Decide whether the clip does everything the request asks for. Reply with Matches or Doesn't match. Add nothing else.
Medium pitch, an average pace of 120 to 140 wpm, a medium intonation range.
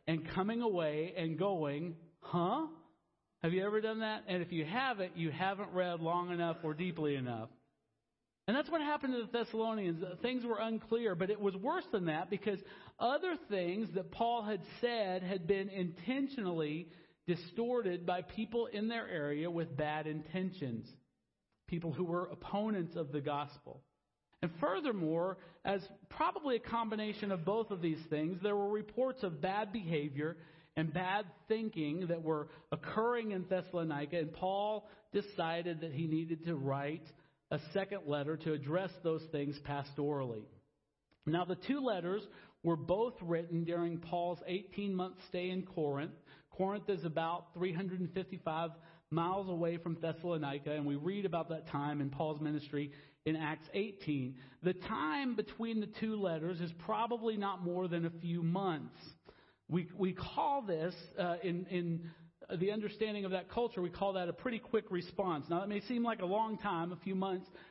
Doesn't match